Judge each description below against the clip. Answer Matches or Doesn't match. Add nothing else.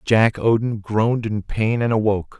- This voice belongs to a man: Matches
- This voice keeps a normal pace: Matches